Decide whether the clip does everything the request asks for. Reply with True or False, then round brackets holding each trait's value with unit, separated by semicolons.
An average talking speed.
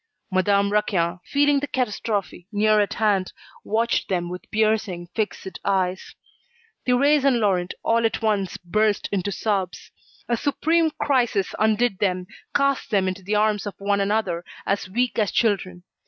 True (150 wpm)